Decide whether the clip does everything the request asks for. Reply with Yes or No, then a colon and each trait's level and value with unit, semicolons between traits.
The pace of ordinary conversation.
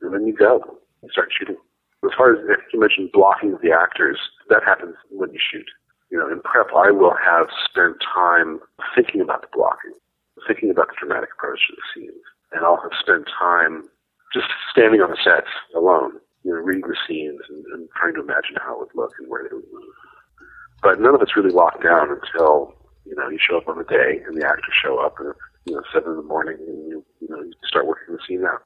No: fast, 230 wpm